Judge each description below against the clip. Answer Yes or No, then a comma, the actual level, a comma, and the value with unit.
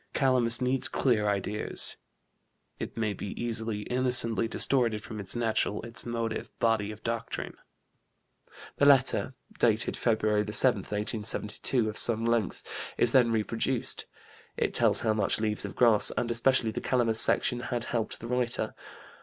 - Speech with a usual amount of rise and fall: No, narrow, 2.1 semitones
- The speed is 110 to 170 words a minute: Yes, average, 145 wpm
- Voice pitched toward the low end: Yes, low, 115 Hz